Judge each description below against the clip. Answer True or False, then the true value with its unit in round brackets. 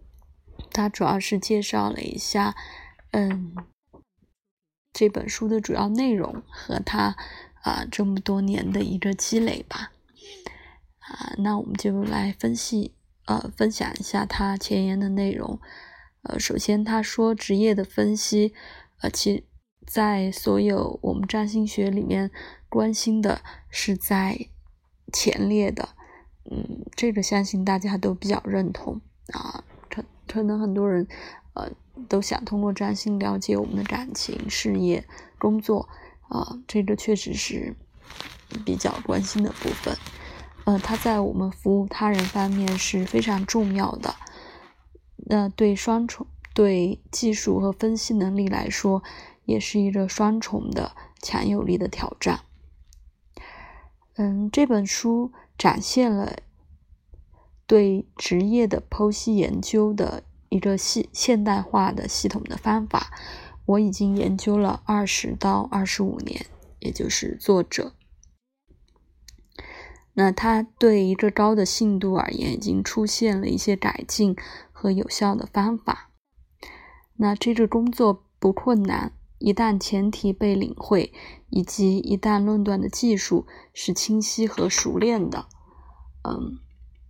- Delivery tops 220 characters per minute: False (190 characters per minute)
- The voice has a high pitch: True (200 Hz)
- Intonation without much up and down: True (2.1 semitones)